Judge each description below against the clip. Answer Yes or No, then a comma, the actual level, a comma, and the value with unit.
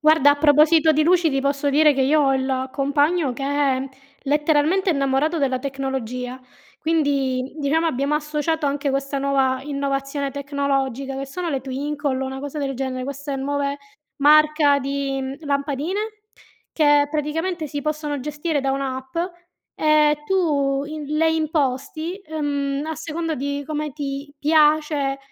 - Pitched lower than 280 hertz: No, very high, 285 Hz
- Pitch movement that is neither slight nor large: No, narrow, 2.0 semitones